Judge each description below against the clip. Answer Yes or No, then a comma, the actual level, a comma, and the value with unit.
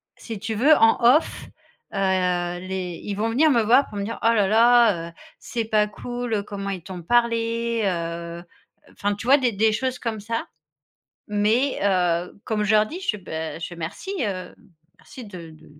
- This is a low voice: No, high, 215 Hz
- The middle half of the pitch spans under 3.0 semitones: No, average, 3.7 semitones